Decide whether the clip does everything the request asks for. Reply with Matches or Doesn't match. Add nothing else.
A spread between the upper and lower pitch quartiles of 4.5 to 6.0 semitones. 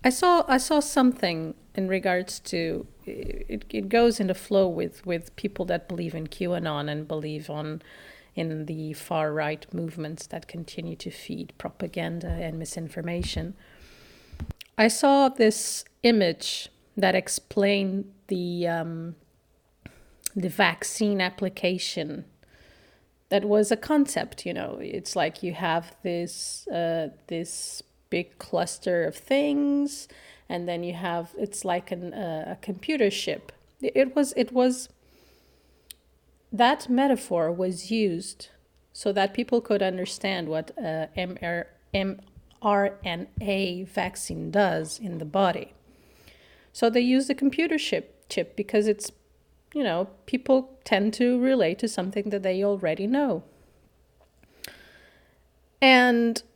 Matches